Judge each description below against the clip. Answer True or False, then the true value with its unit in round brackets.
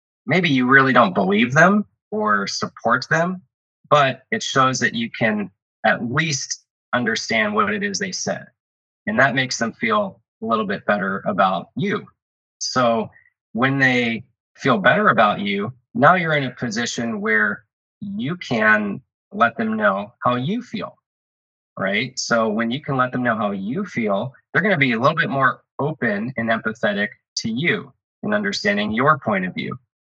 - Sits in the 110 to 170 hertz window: True (135 Hz)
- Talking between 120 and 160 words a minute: False (170 wpm)